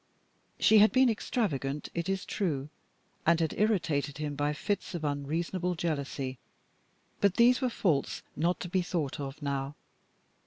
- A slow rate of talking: No, average, 150 wpm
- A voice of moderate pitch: Yes, medium, 165 Hz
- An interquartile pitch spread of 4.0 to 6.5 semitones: Yes, average, 5.2 semitones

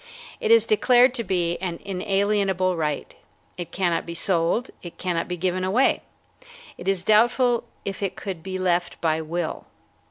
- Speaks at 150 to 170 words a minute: Yes, average, 160 wpm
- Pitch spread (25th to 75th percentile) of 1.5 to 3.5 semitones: Yes, average, 3.2 semitones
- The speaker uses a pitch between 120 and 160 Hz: No, medium, 185 Hz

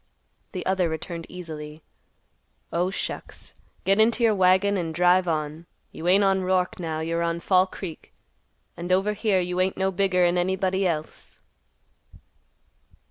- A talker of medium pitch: Yes, medium, 180 Hz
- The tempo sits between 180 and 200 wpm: No, average, 140 wpm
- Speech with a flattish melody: Yes, narrow, 2.2 semitones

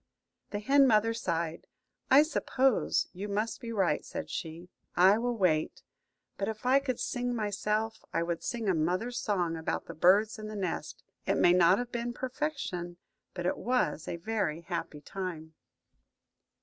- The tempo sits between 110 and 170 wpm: Yes, average, 165 wpm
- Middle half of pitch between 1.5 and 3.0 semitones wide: No, wide, 5.4 semitones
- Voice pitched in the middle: No, high, 205 Hz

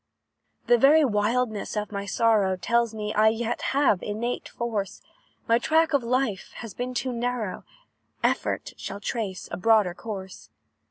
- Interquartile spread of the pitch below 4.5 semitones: Yes, average, 3.0 semitones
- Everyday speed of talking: Yes, average, 150 wpm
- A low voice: No, high, 225 Hz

